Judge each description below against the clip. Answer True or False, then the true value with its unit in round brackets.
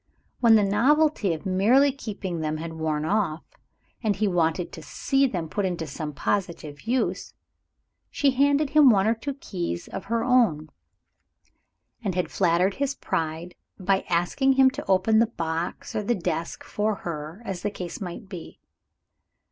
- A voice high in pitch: True (195 Hz)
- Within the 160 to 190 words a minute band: True (165 wpm)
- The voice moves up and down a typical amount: False (5.8 semitones)